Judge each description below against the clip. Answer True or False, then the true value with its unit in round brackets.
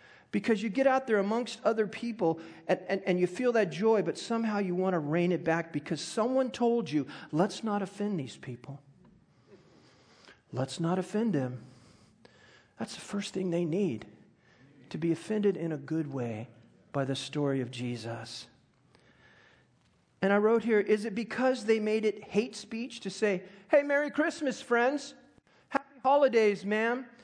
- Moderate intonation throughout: False (5.9 semitones)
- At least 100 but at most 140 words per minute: False (165 wpm)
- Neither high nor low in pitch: False (200 Hz)